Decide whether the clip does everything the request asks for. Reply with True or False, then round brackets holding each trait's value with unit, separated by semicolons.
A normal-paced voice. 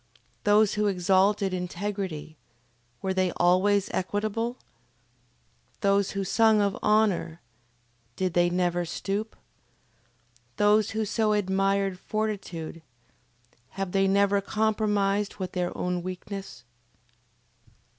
False (100 wpm)